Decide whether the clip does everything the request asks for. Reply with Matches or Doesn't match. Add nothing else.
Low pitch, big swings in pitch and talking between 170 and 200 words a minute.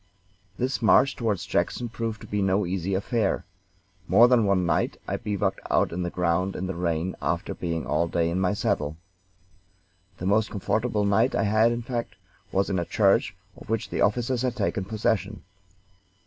Doesn't match